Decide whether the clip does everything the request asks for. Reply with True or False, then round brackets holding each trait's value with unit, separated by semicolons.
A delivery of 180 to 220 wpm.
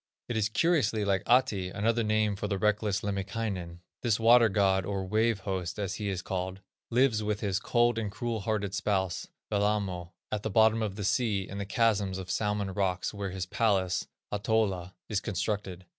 True (185 wpm)